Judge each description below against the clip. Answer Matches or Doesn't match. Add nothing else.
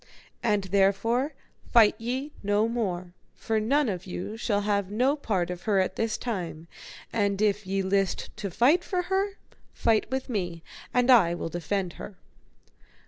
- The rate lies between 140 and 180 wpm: Matches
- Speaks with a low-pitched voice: Doesn't match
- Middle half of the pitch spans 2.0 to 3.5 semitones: Doesn't match